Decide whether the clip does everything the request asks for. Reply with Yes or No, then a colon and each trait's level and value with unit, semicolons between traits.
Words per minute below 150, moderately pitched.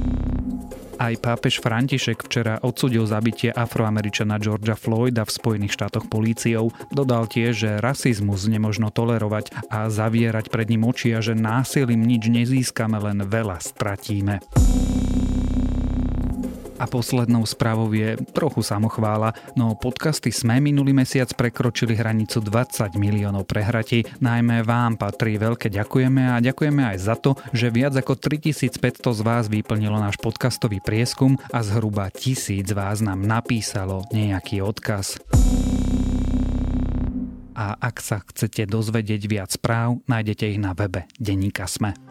No: average, 130 wpm; low, 115 Hz